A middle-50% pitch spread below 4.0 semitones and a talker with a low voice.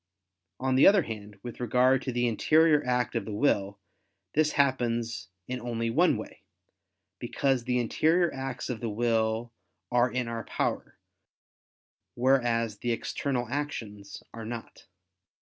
Yes: narrow, 2.6 semitones; low, 120 Hz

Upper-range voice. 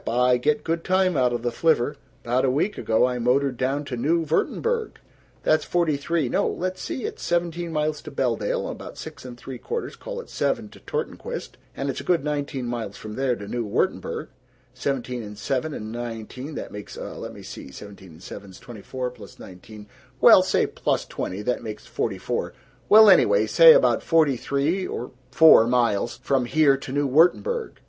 No: low, 135 Hz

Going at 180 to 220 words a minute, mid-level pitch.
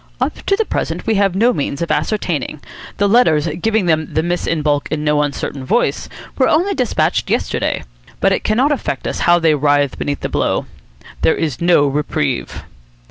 Yes: average, 190 wpm; medium, 165 Hz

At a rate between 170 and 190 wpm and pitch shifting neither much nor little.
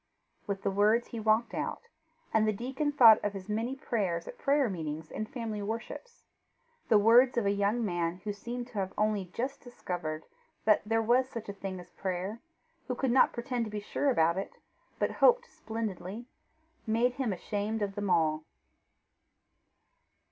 Yes: average, 175 wpm; average, 3.6 semitones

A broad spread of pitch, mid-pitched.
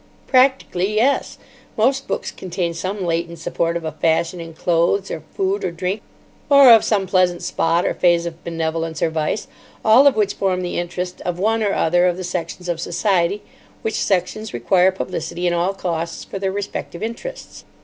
No: average, 3.1 semitones; medium, 180 Hz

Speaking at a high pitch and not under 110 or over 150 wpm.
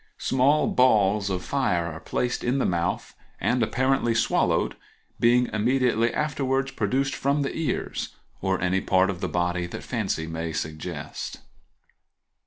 No: low, 110 Hz; average, 140 wpm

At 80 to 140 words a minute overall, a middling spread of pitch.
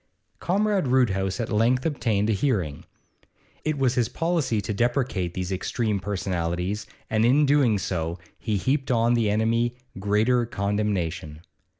Yes: slow, 135 wpm; average, 4.5 semitones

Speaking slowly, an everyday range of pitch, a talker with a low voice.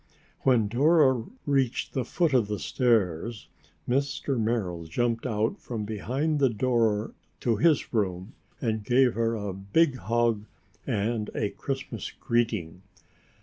Yes: slow, 130 wpm; average, 3.6 semitones; low, 115 Hz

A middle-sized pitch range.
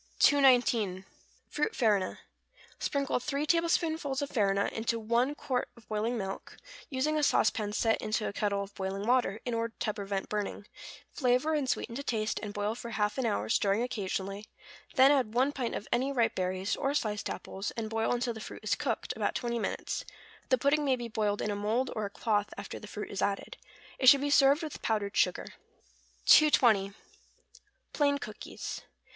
Yes: average, 4.6 semitones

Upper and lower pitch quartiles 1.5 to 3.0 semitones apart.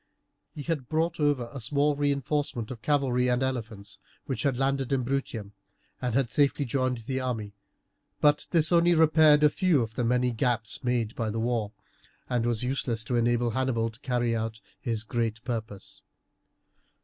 No: average, 3.5 semitones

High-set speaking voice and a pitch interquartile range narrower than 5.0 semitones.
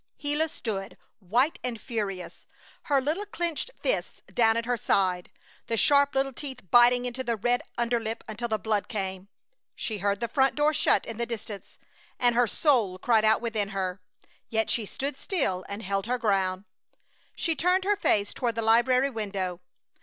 Yes: high, 230 Hz; average, 4.6 semitones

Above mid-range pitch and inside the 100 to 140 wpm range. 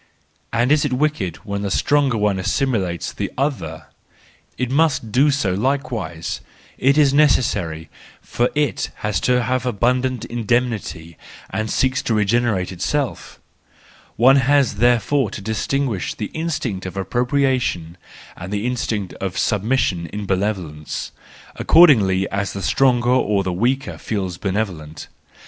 No: low, 115 Hz; slow, 135 wpm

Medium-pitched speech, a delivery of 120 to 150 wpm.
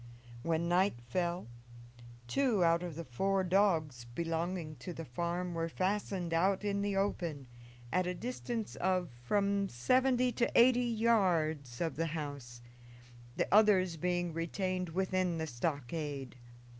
Yes: medium, 175 Hz; slow, 135 wpm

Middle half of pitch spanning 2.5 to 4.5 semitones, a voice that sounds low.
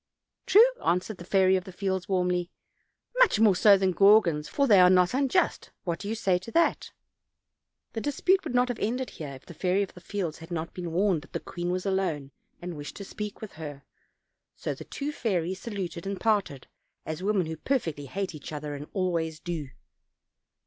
No: average, 3.9 semitones; medium, 185 Hz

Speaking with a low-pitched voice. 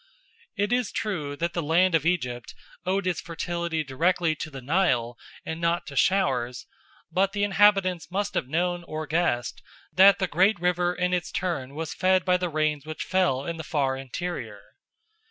No: medium, 170 Hz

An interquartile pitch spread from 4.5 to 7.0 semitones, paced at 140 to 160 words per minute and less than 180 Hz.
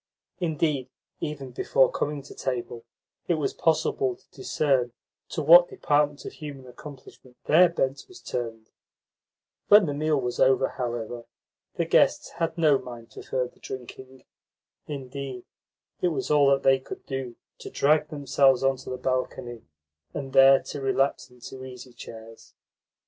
No: average, 2.8 semitones; average, 150 wpm; low, 135 Hz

